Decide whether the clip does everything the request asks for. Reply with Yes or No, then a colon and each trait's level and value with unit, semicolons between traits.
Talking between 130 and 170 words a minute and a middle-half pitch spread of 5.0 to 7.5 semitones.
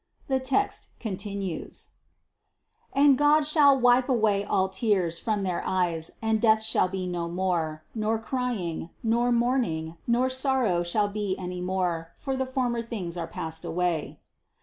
Yes: average, 155 wpm; wide, 5.6 semitones